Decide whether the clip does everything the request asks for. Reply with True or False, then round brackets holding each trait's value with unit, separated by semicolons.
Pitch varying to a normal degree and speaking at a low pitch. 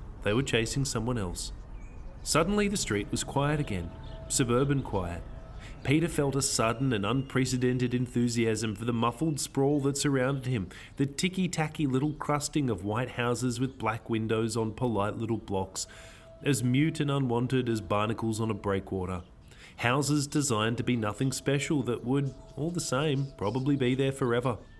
True (3.9 semitones; 125 Hz)